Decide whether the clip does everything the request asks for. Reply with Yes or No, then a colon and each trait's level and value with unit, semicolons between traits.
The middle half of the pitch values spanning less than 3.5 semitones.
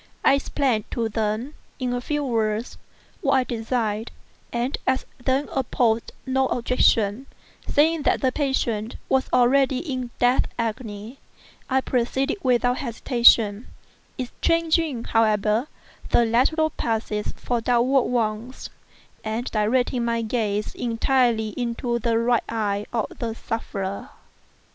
Yes: average, 2.8 semitones